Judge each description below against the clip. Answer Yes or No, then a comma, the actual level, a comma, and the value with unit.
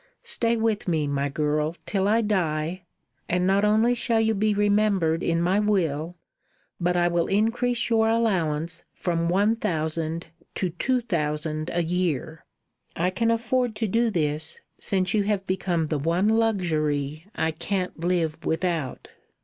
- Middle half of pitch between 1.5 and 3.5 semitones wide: No, average, 4.9 semitones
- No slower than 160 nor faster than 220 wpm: No, average, 150 wpm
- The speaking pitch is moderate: Yes, medium, 180 Hz